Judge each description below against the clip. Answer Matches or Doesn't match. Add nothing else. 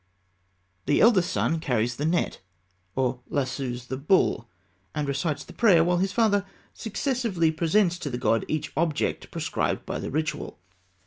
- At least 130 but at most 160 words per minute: Matches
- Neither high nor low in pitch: Matches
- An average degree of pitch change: Doesn't match